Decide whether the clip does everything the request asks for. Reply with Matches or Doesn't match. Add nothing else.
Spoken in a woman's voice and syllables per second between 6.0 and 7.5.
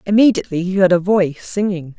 Matches